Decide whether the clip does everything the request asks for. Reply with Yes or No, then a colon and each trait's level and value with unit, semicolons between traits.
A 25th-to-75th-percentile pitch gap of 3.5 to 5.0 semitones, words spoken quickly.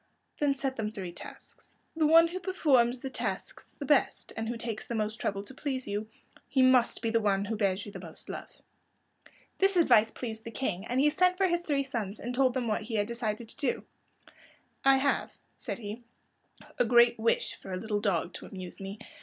Yes: average, 4.2 semitones; fast, 210 wpm